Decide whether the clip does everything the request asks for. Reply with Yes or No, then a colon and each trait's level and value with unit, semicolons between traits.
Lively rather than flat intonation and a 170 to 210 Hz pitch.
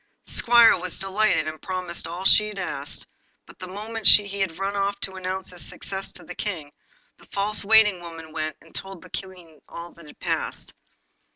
No: average, 3.0 semitones; high, 190 Hz